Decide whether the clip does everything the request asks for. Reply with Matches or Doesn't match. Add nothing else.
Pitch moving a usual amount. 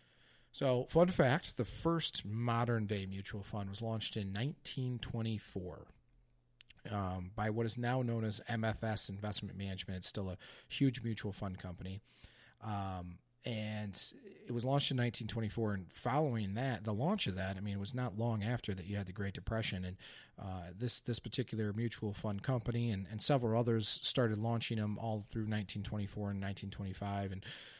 Matches